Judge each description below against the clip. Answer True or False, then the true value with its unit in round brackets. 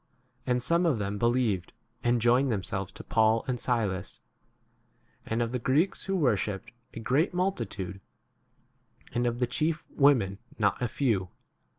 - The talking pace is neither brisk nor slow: True (165 wpm)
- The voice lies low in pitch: True (120 Hz)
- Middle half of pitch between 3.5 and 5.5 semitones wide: True (4.5 semitones)